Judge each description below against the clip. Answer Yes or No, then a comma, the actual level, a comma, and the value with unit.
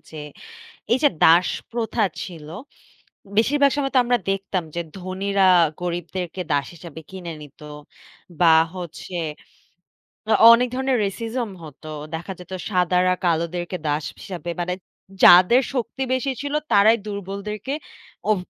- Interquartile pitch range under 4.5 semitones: No, average, 4.8 semitones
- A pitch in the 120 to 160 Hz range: No, high, 190 Hz